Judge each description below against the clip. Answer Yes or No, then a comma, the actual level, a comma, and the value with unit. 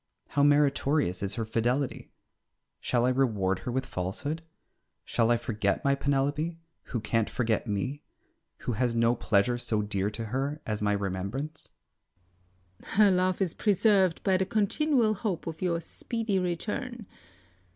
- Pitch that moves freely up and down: Yes, wide, 7.9 semitones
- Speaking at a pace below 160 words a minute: Yes, average, 150 wpm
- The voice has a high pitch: No, low, 135 Hz